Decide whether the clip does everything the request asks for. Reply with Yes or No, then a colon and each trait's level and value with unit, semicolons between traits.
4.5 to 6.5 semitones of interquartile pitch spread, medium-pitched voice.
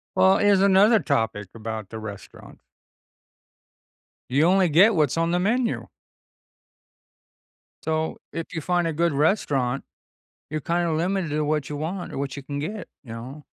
Yes: average, 4.9 semitones; medium, 160 Hz